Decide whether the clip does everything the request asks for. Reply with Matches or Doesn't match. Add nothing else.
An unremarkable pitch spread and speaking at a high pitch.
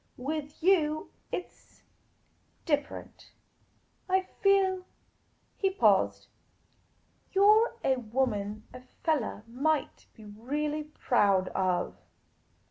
Doesn't match